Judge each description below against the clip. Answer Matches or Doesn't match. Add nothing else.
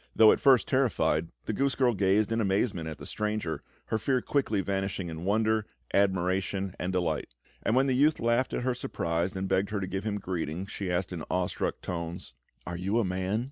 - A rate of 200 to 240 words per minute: Matches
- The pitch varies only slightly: Doesn't match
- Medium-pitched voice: Doesn't match